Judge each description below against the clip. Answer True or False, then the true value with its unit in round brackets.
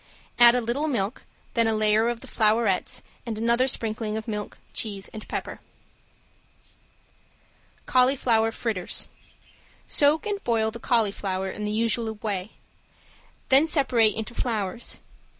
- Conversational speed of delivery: False (130 wpm)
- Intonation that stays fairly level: True (2.1 semitones)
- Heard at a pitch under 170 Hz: False (225 Hz)